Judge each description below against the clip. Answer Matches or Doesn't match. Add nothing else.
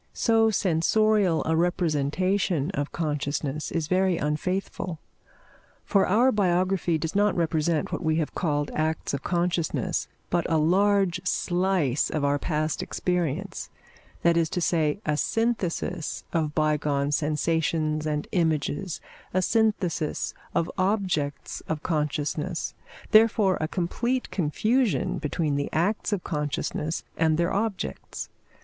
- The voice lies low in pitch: Doesn't match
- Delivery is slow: Matches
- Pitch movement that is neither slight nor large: Matches